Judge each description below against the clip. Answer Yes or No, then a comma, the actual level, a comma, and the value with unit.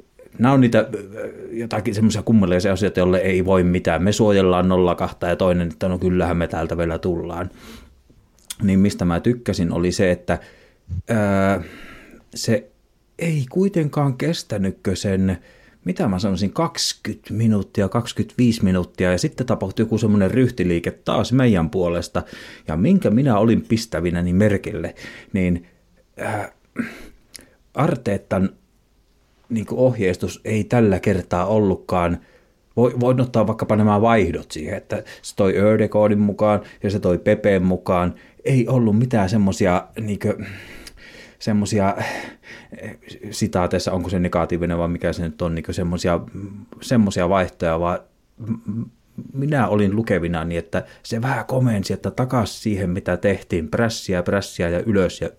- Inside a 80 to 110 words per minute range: No, average, 130 wpm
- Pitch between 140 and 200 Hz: No, low, 100 Hz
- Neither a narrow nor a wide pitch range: Yes, average, 3.8 semitones